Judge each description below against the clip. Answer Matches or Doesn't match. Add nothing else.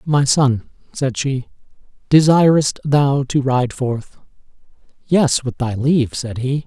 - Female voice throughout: Doesn't match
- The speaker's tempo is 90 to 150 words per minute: Matches